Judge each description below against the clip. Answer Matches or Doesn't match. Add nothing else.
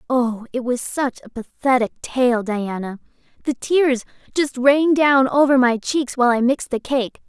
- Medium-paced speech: Matches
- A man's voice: Doesn't match